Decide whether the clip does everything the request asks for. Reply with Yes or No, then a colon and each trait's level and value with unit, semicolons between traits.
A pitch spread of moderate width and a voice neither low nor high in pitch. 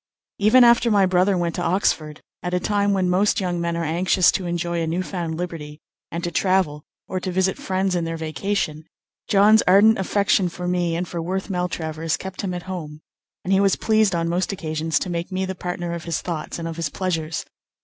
No: narrow, 2.3 semitones; medium, 180 Hz